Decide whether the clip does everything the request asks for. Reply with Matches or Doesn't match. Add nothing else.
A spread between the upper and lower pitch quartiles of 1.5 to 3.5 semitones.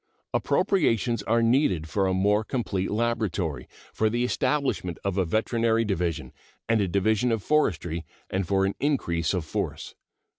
Doesn't match